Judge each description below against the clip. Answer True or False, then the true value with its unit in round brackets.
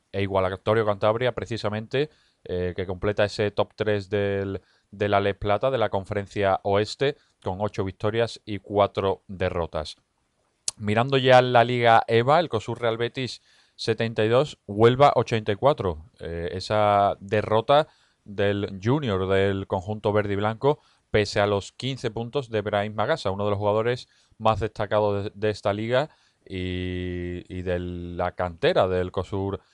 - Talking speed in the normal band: True (150 wpm)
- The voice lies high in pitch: False (105 Hz)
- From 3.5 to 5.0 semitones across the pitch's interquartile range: False (2.8 semitones)